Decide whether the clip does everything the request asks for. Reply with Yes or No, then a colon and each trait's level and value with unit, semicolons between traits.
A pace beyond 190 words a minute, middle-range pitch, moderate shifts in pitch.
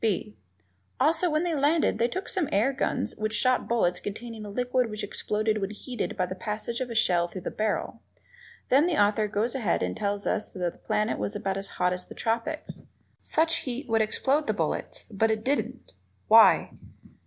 No: average, 200 wpm; high, 220 Hz; average, 4.2 semitones